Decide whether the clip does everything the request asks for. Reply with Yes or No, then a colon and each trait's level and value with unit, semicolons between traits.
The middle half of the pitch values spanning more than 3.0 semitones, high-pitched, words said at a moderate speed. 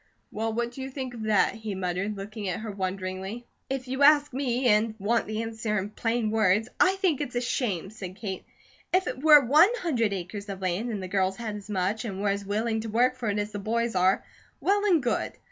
No: average, 3.7 semitones; high, 220 Hz; fast, 230 wpm